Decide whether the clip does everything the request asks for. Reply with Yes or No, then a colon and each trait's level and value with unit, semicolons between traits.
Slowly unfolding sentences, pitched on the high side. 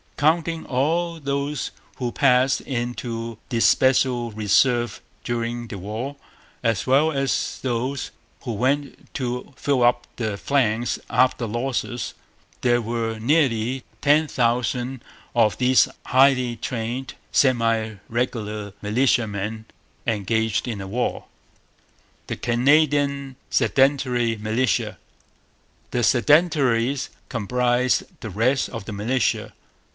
No: slow, 105 wpm; low, 120 Hz